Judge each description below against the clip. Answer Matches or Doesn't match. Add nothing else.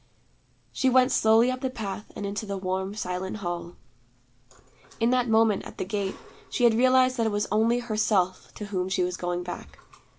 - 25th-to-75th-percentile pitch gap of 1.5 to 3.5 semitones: Doesn't match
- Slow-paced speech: Doesn't match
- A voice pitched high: Matches